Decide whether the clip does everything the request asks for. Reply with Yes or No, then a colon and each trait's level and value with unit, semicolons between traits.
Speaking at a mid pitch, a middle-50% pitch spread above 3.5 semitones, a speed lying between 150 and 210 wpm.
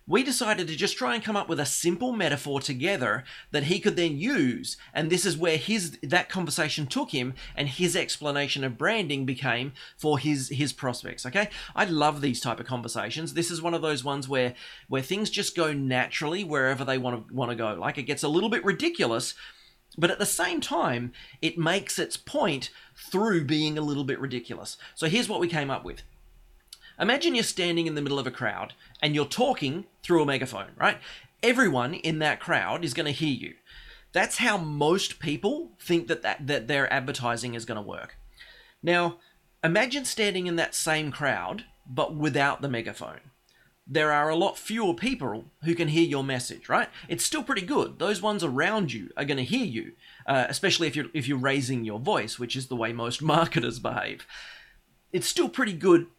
Yes: medium, 155 Hz; average, 5.0 semitones; average, 200 wpm